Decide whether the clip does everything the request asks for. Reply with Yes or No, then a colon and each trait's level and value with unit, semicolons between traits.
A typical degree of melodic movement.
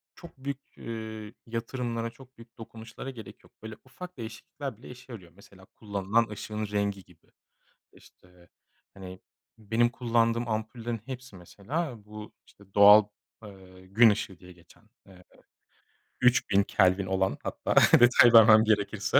Yes: average, 3.2 semitones